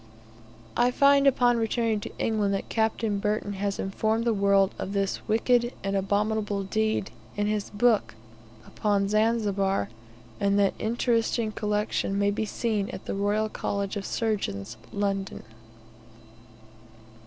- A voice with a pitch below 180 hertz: No, high, 210 Hz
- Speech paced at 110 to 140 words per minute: Yes, slow, 135 wpm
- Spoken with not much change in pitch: Yes, narrow, 2.0 semitones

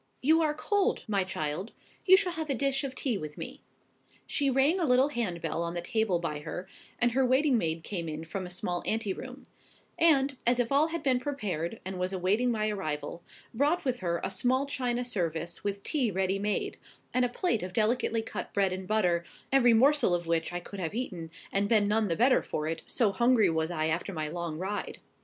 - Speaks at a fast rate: Yes, fast, 215 wpm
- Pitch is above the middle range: Yes, high, 210 Hz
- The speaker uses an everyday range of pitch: No, wide, 6.6 semitones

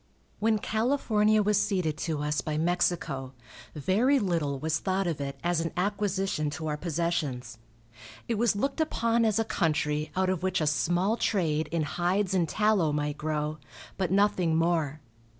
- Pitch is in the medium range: Yes, medium, 175 Hz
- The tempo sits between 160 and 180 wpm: Yes, average, 165 wpm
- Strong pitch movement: No, average, 5.0 semitones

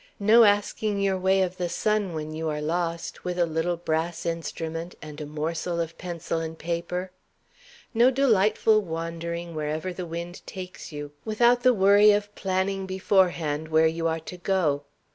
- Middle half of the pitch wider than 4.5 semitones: No, average, 3.1 semitones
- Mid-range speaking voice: Yes, medium, 175 Hz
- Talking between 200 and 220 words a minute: No, average, 165 wpm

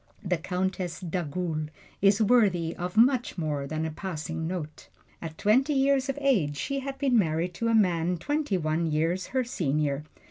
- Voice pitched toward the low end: No, medium, 180 Hz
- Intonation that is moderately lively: No, wide, 6.3 semitones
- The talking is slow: No, average, 170 wpm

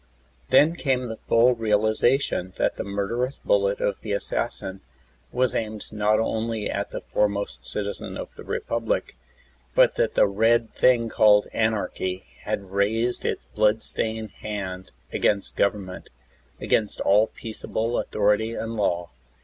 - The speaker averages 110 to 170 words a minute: Yes, average, 140 wpm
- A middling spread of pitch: No, narrow, 2.2 semitones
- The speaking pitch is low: Yes, low, 110 Hz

